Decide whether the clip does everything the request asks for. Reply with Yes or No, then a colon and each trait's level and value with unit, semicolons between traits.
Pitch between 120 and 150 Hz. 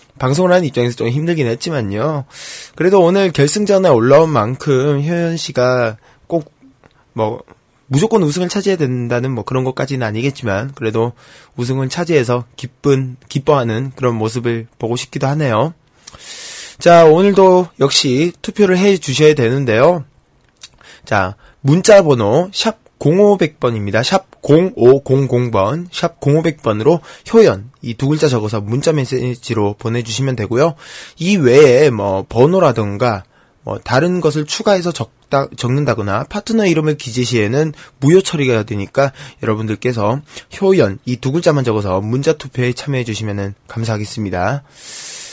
Yes: low, 135 Hz